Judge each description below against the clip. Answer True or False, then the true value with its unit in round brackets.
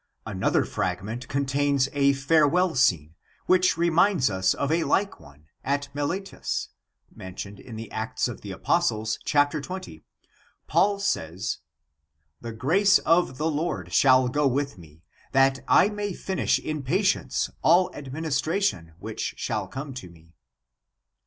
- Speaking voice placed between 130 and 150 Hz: True (140 Hz)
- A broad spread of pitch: True (8.0 semitones)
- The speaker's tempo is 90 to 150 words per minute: True (140 wpm)